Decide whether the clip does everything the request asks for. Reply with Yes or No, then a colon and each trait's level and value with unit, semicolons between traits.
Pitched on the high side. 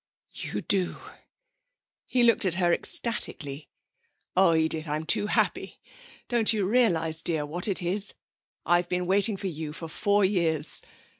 No: medium, 180 Hz